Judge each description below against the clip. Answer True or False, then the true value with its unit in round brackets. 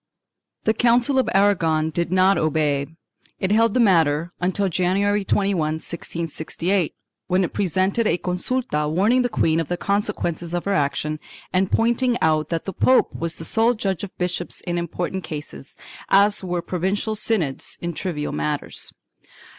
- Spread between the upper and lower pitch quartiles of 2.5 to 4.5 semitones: True (4.0 semitones)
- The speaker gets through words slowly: False (155 wpm)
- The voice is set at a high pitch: False (180 Hz)